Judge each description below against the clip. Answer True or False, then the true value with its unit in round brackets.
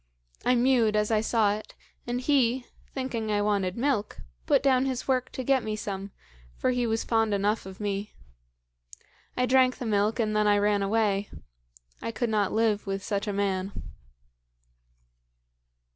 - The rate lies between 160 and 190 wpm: True (165 wpm)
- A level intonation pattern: False (3.3 semitones)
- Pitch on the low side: False (215 Hz)